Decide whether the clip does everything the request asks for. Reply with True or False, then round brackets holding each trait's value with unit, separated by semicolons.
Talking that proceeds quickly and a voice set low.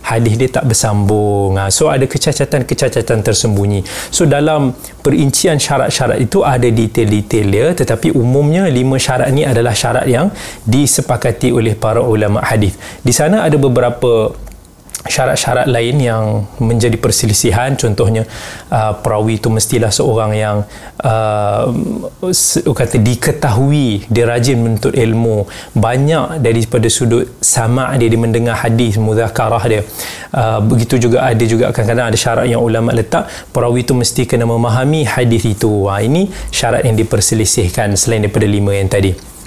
False (140 wpm; 115 Hz)